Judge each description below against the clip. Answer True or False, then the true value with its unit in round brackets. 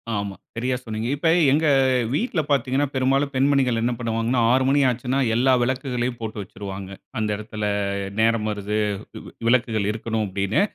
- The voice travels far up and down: False (3.4 semitones)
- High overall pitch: False (120 Hz)